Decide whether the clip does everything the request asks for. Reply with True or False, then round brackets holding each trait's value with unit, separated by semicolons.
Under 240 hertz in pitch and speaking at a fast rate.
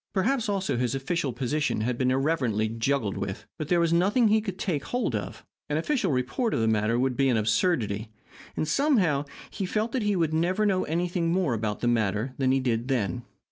True (140 Hz; 210 wpm)